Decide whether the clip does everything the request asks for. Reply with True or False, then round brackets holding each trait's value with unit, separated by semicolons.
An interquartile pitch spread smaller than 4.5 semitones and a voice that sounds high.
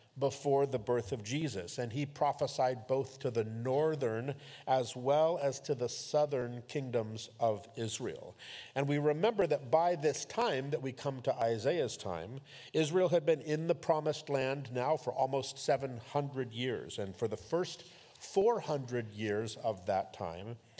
False (3.6 semitones; 135 Hz)